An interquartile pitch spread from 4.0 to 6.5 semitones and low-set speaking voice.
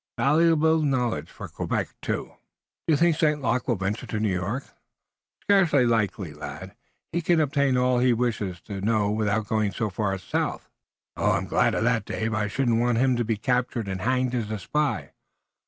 Yes: average, 4.6 semitones; low, 120 Hz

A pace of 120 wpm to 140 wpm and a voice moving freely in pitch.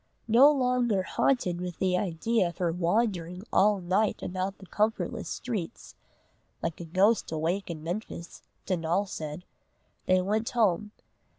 No: slow, 135 wpm; average, 3.9 semitones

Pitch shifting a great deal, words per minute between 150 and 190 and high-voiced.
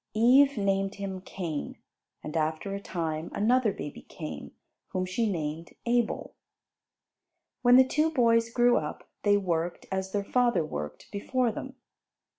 No: wide, 6.1 semitones; average, 140 wpm; high, 200 Hz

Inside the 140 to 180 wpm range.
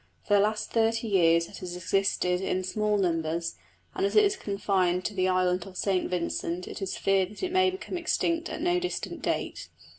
No: fast, 205 wpm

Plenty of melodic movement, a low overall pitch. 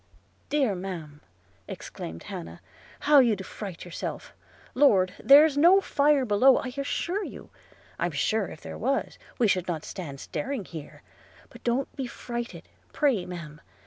No: wide, 7.7 semitones; high, 220 Hz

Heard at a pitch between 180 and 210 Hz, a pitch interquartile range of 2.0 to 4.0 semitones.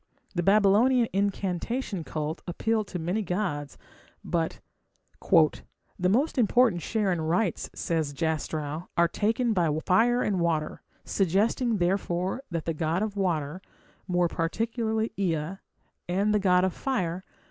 No: medium, 185 Hz; average, 4.4 semitones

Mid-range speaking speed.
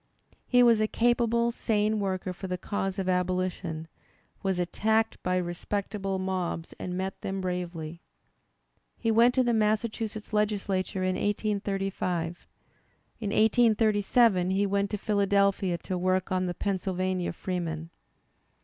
No: slow, 130 wpm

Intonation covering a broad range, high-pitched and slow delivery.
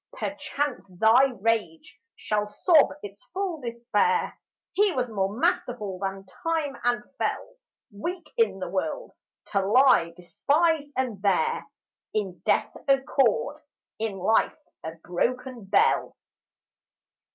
Yes: wide, 6.7 semitones; high, 240 Hz; slow, 120 wpm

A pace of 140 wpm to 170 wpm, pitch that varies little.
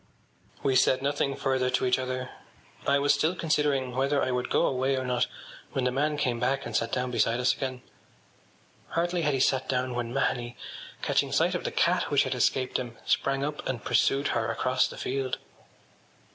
No: average, 200 wpm; narrow, 1.7 semitones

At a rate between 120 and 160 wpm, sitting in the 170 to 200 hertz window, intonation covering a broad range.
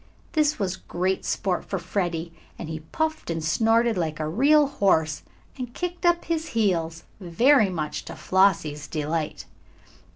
Yes: average, 150 wpm; medium, 185 Hz; wide, 7.3 semitones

